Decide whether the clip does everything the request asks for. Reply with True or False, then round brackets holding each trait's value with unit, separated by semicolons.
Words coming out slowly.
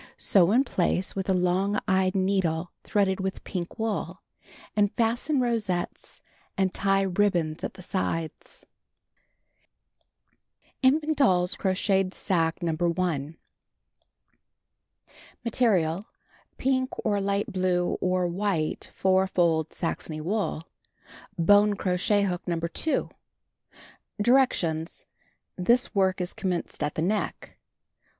True (105 wpm)